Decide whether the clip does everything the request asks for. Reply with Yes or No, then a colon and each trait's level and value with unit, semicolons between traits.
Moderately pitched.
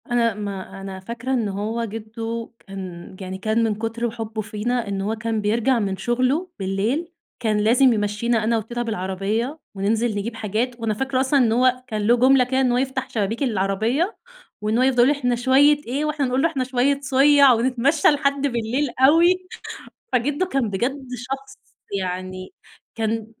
No: high, 235 Hz